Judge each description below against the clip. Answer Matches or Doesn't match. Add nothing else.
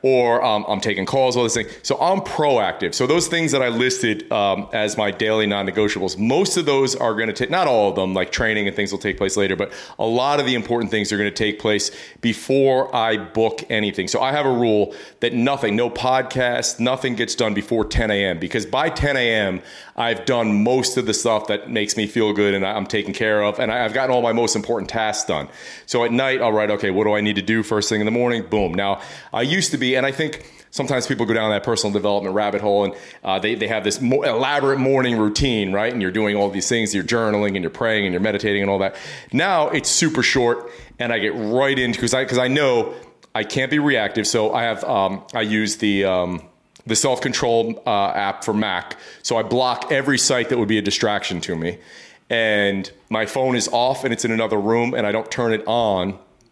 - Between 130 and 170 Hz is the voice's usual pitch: Doesn't match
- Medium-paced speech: Doesn't match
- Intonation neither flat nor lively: Matches